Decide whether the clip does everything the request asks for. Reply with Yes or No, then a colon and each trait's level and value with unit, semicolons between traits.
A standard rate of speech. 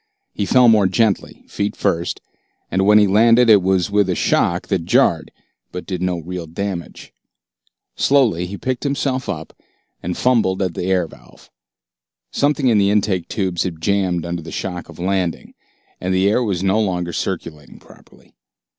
Yes: average, 170 wpm